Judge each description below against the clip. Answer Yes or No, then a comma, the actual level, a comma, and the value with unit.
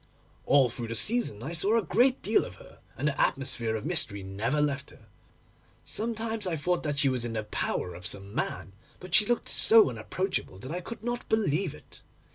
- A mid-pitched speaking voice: Yes, medium, 145 Hz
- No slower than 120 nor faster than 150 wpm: No, fast, 205 wpm